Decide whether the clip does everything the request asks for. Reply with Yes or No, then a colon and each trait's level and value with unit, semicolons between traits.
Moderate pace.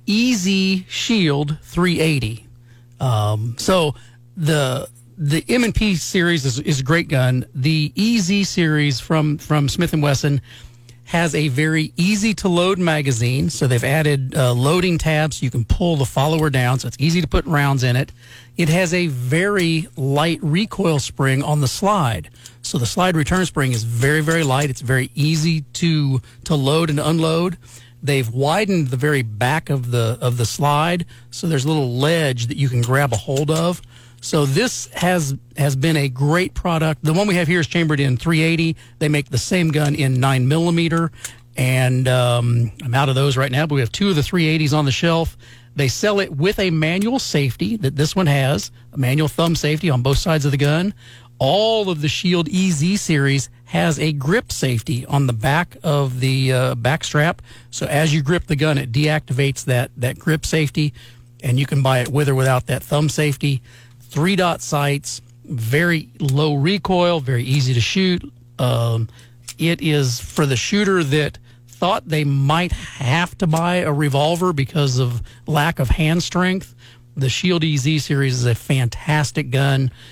Yes: average, 180 wpm